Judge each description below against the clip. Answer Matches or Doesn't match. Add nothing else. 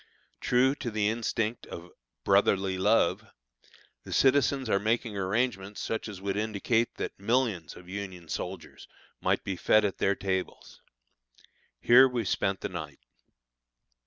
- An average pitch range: Matches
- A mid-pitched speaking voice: Doesn't match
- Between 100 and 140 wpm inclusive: Matches